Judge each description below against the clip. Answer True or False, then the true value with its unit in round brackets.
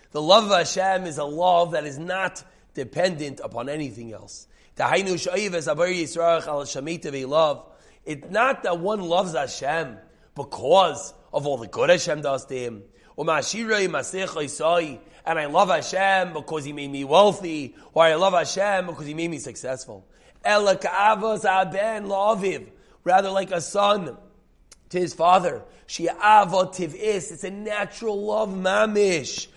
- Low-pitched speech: False (175 Hz)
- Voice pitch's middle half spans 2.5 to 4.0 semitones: False (4.8 semitones)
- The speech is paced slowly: True (120 wpm)